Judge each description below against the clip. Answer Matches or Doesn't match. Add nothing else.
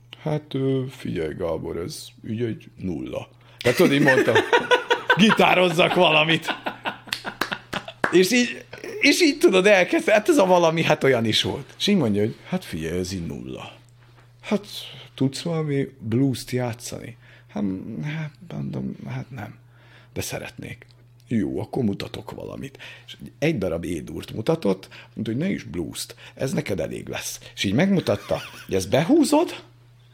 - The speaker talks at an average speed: Matches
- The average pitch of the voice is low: Matches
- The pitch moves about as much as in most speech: Doesn't match